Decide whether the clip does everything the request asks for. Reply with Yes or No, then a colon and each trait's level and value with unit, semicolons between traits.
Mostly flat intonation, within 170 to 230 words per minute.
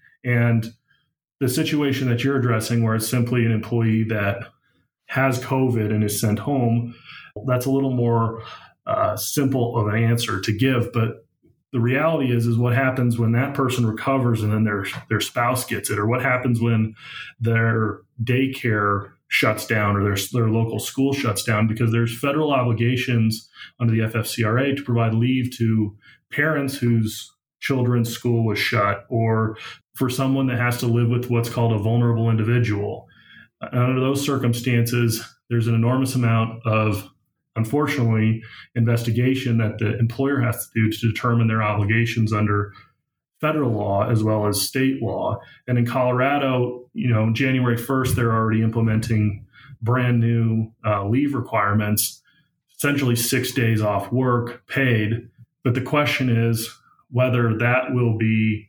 No: narrow, 2.3 semitones; average, 150 wpm